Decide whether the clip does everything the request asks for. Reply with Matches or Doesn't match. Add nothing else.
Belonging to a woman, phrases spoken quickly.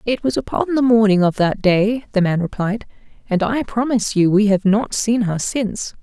Matches